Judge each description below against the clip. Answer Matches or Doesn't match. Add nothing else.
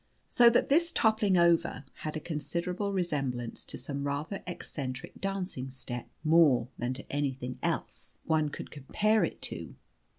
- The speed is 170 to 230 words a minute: Doesn't match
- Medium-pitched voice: Matches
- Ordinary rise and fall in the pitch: Doesn't match